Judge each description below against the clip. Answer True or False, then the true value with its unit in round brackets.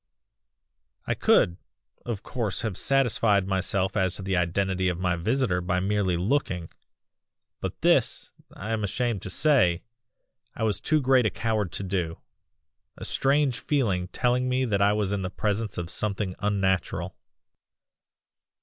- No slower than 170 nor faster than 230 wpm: False (150 wpm)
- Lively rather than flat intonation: False (4.0 semitones)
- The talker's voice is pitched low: True (100 Hz)